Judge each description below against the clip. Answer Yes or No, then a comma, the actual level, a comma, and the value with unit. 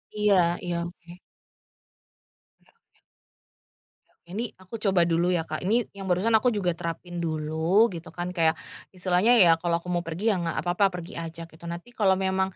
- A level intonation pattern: Yes, narrow, 2.3 semitones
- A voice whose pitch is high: No, medium, 175 Hz